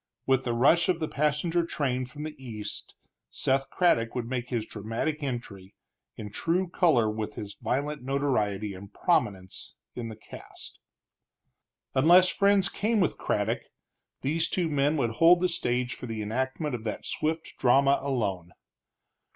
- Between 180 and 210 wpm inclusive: No, average, 150 wpm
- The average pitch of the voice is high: No, low, 130 Hz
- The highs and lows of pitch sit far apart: Yes, wide, 5.8 semitones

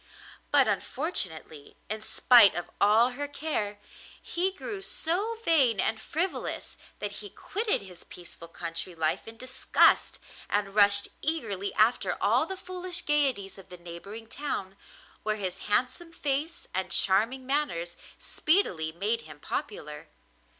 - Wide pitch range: Yes, wide, 7.8 semitones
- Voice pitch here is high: Yes, high, 220 Hz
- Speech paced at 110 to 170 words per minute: Yes, slow, 135 wpm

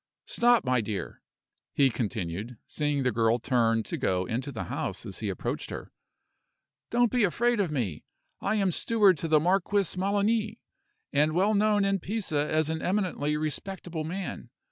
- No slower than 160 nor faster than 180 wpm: Yes, average, 165 wpm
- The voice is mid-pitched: Yes, medium, 160 Hz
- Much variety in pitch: Yes, wide, 8.0 semitones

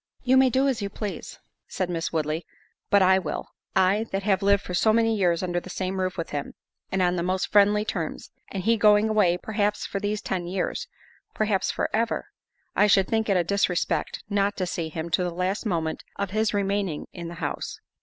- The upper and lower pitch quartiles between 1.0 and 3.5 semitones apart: Yes, average, 2.8 semitones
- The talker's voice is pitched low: No, high, 195 Hz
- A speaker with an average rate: No, fast, 215 wpm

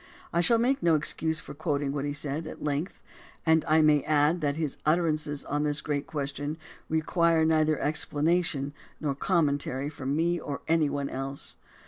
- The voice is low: No, medium, 150 Hz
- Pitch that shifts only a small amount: Yes, narrow, 2.0 semitones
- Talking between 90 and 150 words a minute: No, average, 170 wpm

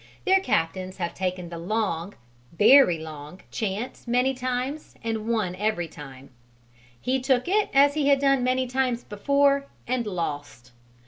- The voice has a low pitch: No, high, 225 Hz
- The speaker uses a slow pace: No, average, 145 wpm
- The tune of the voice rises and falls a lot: Yes, wide, 7.1 semitones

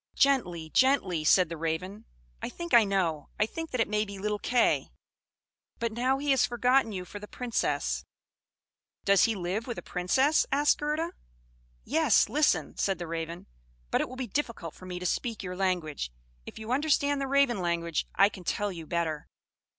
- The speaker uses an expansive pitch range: Yes, wide, 6.6 semitones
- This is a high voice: Yes, high, 210 Hz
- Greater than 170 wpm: Yes, average, 185 wpm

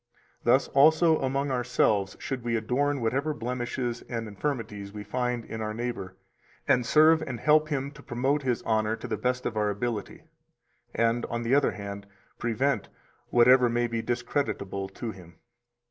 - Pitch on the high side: No, low, 120 Hz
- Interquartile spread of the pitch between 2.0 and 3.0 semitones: No, average, 3.6 semitones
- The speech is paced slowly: No, average, 165 wpm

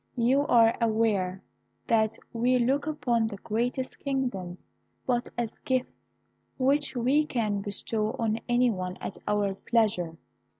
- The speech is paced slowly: Yes, slow, 130 wpm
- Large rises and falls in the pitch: No, average, 3.3 semitones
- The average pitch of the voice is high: Yes, high, 230 Hz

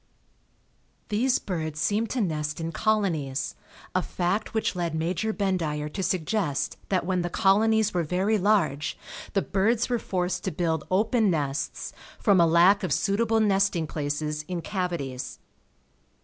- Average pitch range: Yes, average, 4.7 semitones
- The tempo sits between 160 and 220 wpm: No, average, 145 wpm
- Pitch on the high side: No, medium, 180 Hz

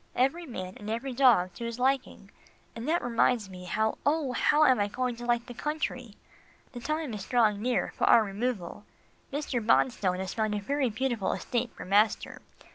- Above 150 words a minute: Yes, average, 185 wpm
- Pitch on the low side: No, high, 235 Hz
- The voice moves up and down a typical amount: Yes, average, 3.8 semitones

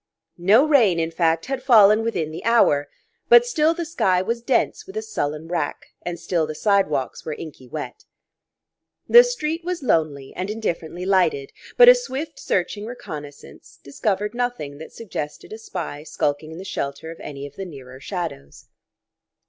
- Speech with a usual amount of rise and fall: No, wide, 8.2 semitones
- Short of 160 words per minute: No, average, 165 wpm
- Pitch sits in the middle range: Yes, medium, 180 Hz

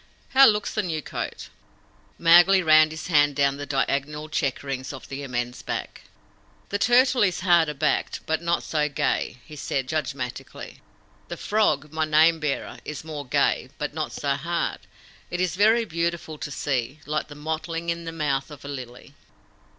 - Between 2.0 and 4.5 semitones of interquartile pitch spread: Yes, average, 3.2 semitones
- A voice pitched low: No, medium, 155 Hz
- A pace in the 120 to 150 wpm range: No, average, 170 wpm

